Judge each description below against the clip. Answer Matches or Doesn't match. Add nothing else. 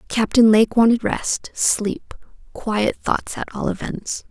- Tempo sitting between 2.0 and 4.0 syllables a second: Matches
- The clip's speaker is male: Doesn't match